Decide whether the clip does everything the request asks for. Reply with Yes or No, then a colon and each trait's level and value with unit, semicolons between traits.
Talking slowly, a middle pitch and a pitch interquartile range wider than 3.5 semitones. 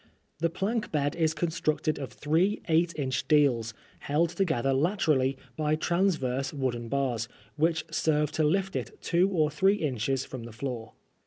No: average, 155 wpm; medium, 150 Hz; average, 4.2 semitones